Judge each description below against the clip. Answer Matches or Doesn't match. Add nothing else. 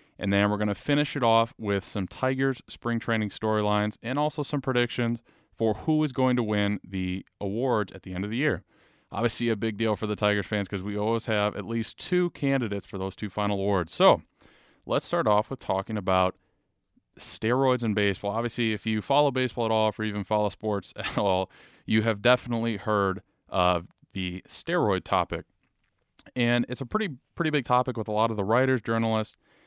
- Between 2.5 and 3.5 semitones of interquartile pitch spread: Matches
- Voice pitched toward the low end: Matches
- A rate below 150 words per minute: Doesn't match